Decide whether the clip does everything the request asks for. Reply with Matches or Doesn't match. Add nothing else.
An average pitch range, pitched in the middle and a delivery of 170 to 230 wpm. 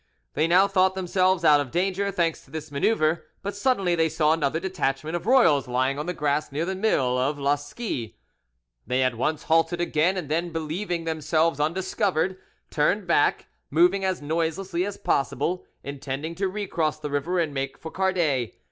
Matches